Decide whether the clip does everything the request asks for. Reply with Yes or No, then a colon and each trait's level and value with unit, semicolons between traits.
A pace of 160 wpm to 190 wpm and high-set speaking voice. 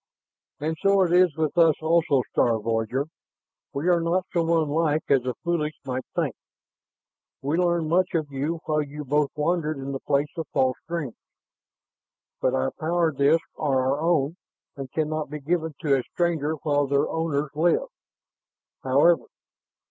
No: average, 165 wpm; medium, 155 Hz